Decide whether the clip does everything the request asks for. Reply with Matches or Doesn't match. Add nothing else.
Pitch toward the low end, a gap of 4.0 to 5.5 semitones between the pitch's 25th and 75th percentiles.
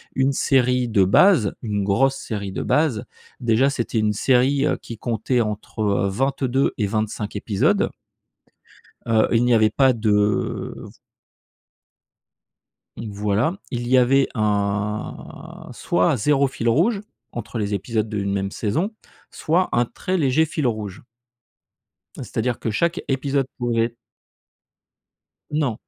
Matches